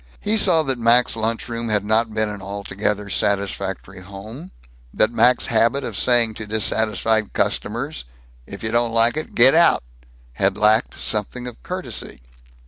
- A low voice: Yes, low, 110 Hz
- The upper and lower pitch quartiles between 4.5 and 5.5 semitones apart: No, average, 2.7 semitones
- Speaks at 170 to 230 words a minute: No, average, 155 wpm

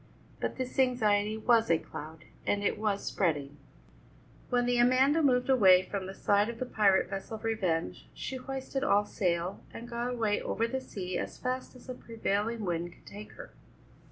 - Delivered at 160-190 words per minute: Yes, average, 180 wpm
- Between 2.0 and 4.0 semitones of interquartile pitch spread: No, average, 4.4 semitones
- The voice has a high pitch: Yes, high, 220 Hz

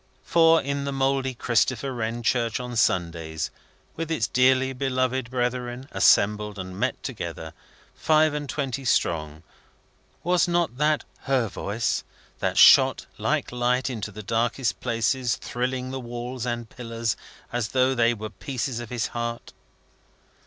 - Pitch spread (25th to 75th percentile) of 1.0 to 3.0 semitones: Yes, narrow, 2.6 semitones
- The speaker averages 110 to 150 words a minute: Yes, average, 140 wpm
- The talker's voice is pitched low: Yes, low, 125 Hz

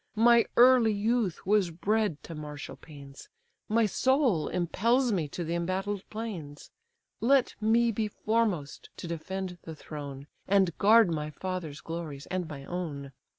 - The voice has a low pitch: No, medium, 185 Hz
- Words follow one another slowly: No, average, 145 wpm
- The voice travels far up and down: Yes, wide, 5.9 semitones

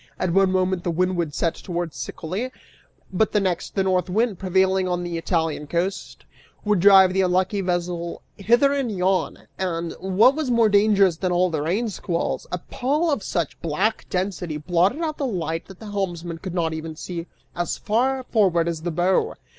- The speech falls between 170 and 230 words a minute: Yes, average, 185 wpm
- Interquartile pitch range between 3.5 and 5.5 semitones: No, average, 2.9 semitones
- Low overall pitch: No, medium, 185 Hz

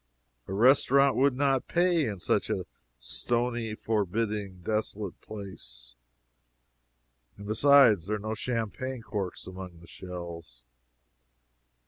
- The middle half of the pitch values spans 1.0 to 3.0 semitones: No, average, 5.1 semitones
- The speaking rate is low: Yes, slow, 110 wpm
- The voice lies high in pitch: No, low, 105 Hz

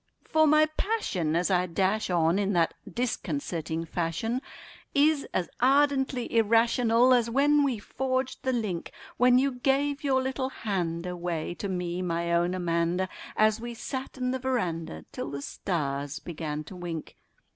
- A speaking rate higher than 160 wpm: No, average, 155 wpm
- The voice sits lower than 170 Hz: No, high, 205 Hz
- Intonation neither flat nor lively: No, wide, 7.2 semitones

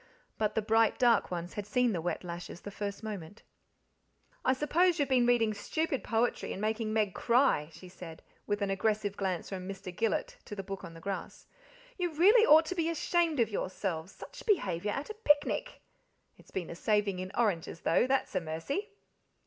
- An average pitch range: No, wide, 6.5 semitones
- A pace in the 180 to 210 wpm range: Yes, average, 190 wpm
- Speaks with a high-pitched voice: Yes, high, 215 Hz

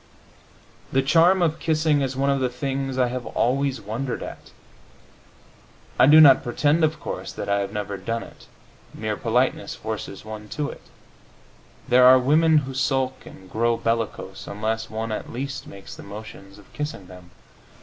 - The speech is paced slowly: No, average, 170 wpm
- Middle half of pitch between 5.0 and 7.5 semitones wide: No, average, 4.3 semitones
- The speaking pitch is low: Yes, low, 125 Hz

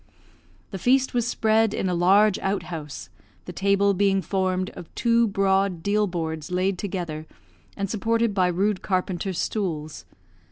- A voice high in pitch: Yes, high, 195 Hz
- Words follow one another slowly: No, average, 145 wpm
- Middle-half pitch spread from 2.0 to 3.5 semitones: Yes, narrow, 2.6 semitones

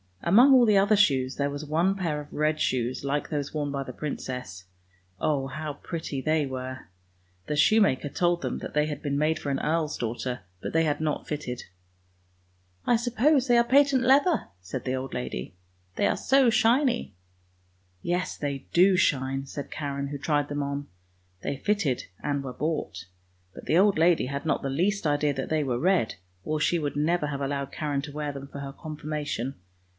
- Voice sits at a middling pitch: Yes, medium, 145 Hz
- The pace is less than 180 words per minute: No, average, 200 wpm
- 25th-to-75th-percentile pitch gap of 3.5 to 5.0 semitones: Yes, average, 4.1 semitones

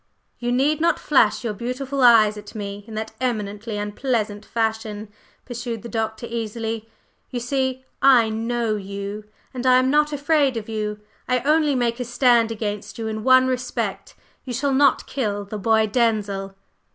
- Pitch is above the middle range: Yes, high, 230 Hz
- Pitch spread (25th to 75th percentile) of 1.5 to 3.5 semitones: Yes, average, 3.2 semitones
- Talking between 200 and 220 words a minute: No, average, 165 wpm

